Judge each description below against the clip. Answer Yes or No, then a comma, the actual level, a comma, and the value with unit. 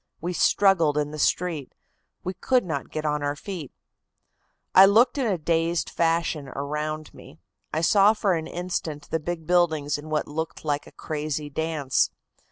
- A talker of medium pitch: Yes, medium, 160 Hz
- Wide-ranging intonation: No, average, 3.0 semitones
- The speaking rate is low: No, average, 170 wpm